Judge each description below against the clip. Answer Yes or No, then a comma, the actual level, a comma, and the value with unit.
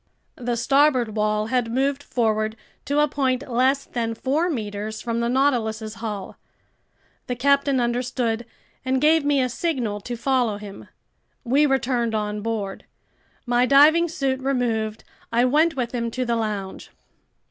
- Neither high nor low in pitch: No, high, 245 Hz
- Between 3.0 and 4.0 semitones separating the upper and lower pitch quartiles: Yes, average, 3.5 semitones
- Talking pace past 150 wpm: No, average, 145 wpm